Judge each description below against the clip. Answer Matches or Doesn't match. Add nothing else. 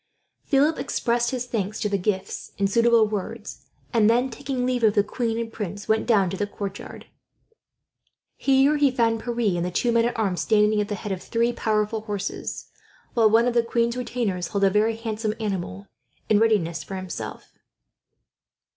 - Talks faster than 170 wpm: Matches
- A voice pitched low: Doesn't match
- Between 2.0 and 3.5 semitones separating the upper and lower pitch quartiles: Matches